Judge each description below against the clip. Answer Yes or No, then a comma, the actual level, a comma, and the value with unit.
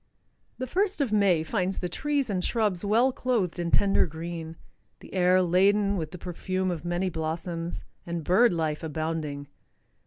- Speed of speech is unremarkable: Yes, average, 160 wpm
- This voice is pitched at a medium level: Yes, medium, 180 Hz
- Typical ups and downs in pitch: Yes, average, 3.6 semitones